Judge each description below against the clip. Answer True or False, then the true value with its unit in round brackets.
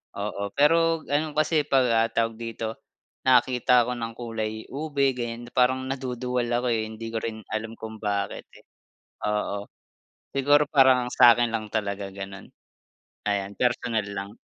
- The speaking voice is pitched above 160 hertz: False (115 Hz)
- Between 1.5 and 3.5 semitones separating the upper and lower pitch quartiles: True (3.1 semitones)